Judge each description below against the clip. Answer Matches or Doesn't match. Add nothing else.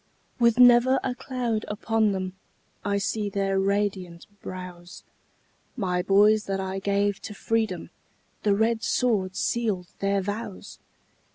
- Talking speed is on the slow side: Matches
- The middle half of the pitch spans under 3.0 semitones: Matches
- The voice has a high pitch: Matches